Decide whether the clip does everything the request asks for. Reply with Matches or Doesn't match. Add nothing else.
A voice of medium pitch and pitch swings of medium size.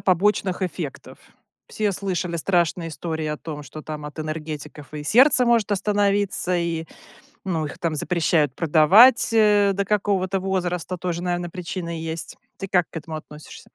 Matches